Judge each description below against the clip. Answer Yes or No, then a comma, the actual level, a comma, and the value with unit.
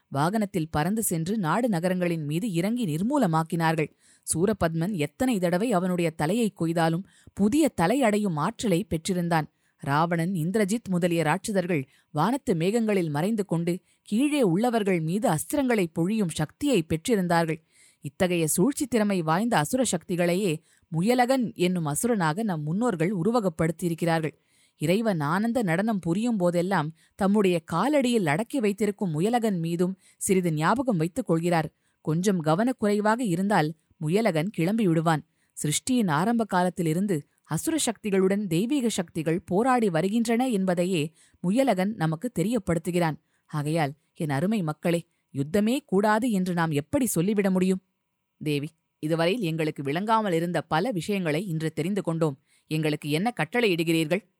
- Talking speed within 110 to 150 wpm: Yes, average, 115 wpm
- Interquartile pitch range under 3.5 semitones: No, average, 4.6 semitones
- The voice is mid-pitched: Yes, medium, 180 Hz